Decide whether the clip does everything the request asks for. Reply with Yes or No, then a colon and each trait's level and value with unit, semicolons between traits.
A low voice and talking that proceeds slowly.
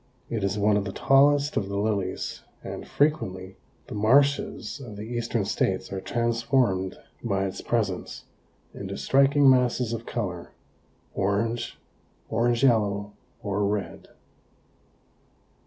Yes: low, 110 Hz; slow, 125 wpm